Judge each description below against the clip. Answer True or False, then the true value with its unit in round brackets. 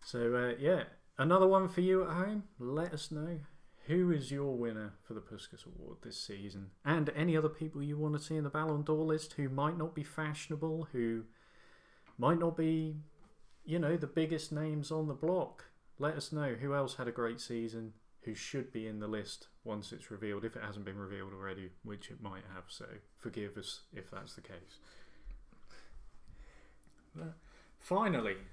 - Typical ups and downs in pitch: False (6.4 semitones)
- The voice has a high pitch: False (140 Hz)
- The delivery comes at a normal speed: True (185 wpm)